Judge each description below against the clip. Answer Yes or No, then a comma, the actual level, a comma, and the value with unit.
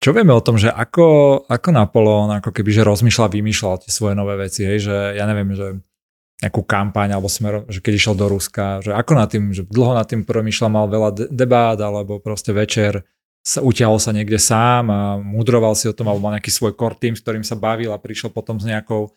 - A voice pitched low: Yes, low, 110 Hz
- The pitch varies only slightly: Yes, narrow, 1.9 semitones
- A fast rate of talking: Yes, fast, 225 wpm